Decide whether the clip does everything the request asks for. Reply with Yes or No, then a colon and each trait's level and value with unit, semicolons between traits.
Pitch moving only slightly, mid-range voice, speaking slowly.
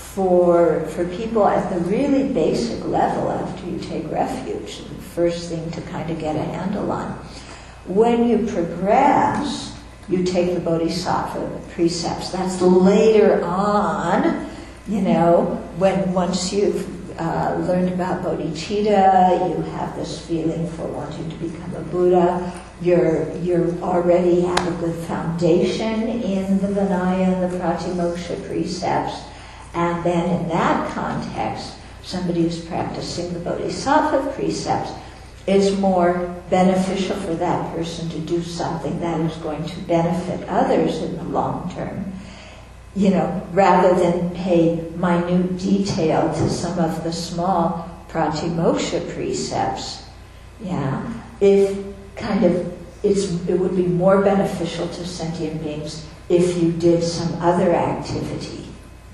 Yes: narrow, 2.1 semitones; medium, 175 Hz; slow, 130 wpm